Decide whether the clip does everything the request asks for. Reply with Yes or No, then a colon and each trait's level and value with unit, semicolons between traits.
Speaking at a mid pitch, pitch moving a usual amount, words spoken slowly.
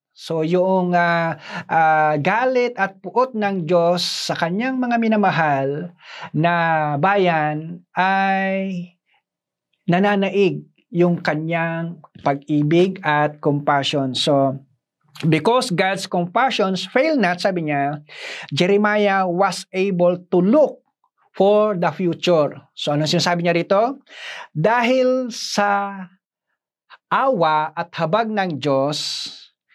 Yes: medium, 180 Hz; average, 4.0 semitones; slow, 100 wpm